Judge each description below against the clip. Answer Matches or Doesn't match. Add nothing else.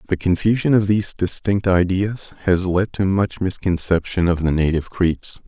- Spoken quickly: Doesn't match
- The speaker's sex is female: Doesn't match